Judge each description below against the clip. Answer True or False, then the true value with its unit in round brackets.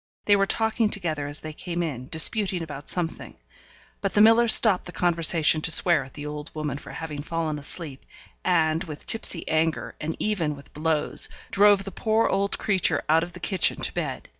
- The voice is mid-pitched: True (165 Hz)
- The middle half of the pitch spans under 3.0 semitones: False (4.3 semitones)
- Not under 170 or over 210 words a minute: True (190 wpm)